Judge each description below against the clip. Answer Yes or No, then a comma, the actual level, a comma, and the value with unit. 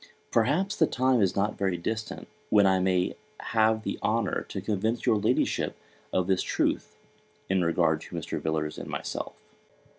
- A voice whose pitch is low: Yes, low, 100 Hz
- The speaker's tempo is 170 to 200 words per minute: No, average, 160 wpm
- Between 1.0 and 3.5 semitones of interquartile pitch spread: Yes, average, 3.2 semitones